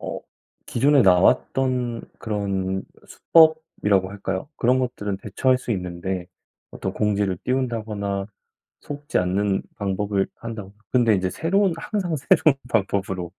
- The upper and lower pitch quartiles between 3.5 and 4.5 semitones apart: No, average, 5.1 semitones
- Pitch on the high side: No, low, 105 Hz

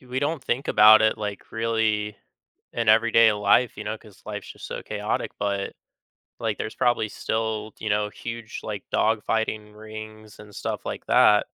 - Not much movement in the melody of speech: Yes, narrow, 1.3 semitones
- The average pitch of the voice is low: Yes, low, 110 Hz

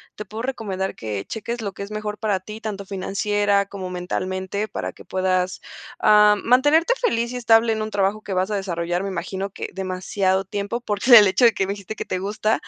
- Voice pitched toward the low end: No, high, 200 Hz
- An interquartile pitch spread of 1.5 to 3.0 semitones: Yes, narrow, 2.4 semitones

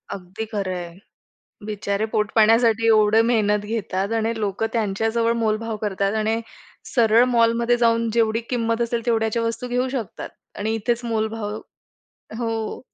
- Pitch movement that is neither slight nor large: No, narrow, 1.5 semitones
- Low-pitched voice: No, high, 225 Hz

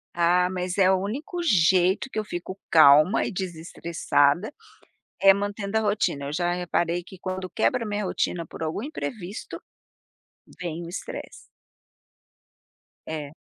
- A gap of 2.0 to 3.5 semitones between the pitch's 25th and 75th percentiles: Yes, average, 3.1 semitones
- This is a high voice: No, medium, 180 Hz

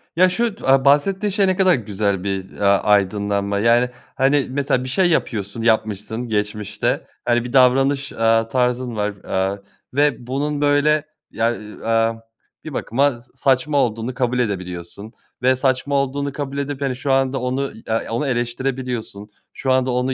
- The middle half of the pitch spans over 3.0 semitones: Yes, average, 4.0 semitones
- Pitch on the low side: Yes, low, 125 Hz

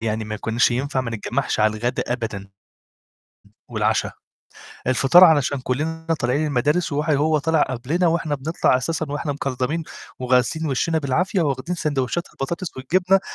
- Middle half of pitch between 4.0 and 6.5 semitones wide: Yes, average, 4.3 semitones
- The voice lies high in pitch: No, medium, 140 Hz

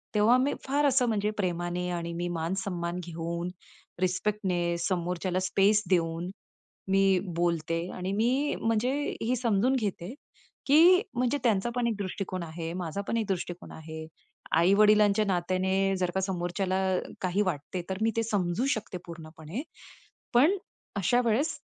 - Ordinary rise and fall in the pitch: Yes, average, 4.0 semitones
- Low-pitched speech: No, high, 190 Hz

